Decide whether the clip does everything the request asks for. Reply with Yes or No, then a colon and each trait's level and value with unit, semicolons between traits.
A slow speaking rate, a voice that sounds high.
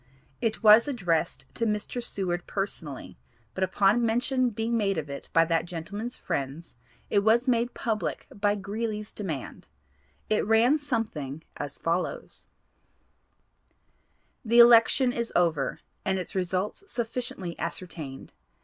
Yes: slow, 125 wpm; high, 205 Hz